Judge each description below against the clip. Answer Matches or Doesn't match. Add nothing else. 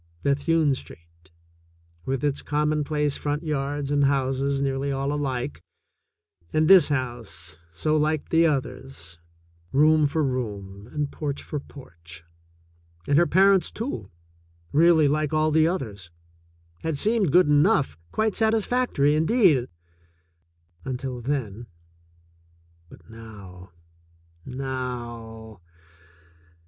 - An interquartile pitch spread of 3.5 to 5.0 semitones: Matches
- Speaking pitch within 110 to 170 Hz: Matches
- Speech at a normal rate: Doesn't match